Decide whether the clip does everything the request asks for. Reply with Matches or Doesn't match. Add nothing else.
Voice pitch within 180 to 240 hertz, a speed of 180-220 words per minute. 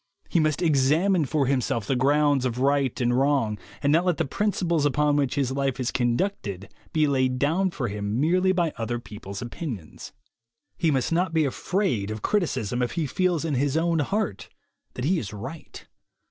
Doesn't match